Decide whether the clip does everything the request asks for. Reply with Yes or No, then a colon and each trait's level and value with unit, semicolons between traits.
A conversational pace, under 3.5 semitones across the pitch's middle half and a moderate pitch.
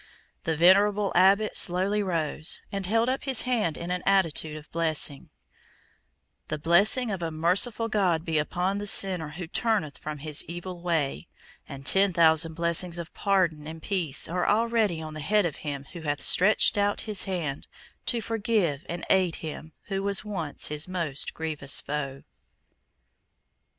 No: average, 160 wpm; average, 4.2 semitones; medium, 175 Hz